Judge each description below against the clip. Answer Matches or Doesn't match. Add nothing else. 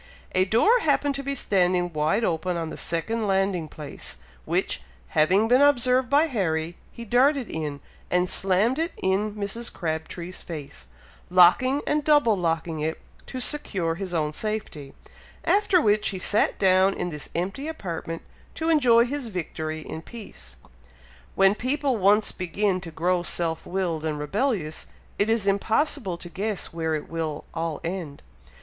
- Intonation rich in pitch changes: Matches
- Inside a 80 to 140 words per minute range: Doesn't match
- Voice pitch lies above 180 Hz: Matches